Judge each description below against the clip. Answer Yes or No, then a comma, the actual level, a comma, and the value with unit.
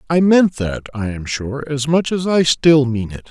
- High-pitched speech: No, medium, 145 Hz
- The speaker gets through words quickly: Yes, fast, 235 wpm